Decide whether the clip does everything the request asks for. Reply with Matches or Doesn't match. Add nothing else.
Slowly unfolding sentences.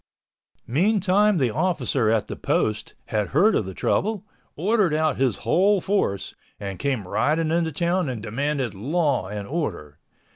Doesn't match